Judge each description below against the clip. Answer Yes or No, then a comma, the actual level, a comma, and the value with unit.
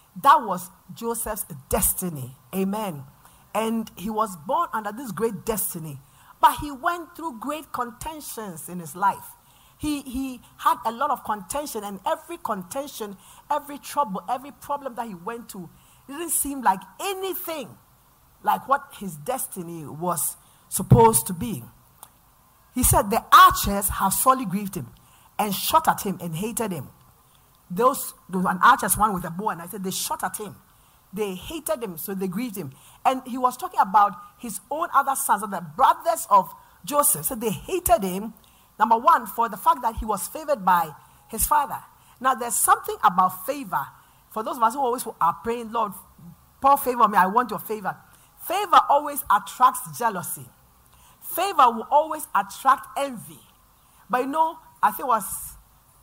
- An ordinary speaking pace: Yes, average, 170 wpm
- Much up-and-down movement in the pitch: Yes, wide, 6.9 semitones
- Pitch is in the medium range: No, high, 230 Hz